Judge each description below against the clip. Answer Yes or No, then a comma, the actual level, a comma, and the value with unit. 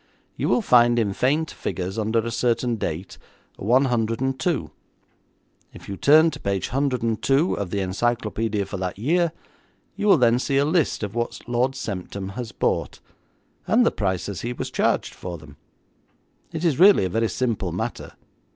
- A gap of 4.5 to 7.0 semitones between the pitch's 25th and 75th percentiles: Yes, average, 5.2 semitones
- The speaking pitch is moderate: No, low, 120 Hz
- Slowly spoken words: No, average, 160 wpm